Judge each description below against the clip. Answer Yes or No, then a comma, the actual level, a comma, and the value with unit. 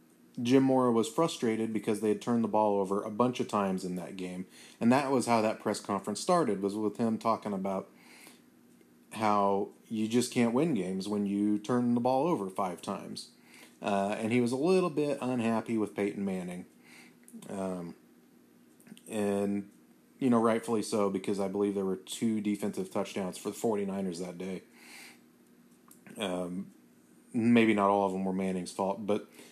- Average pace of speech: Yes, average, 175 wpm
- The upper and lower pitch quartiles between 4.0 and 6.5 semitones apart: No, average, 3.3 semitones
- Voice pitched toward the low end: Yes, low, 105 Hz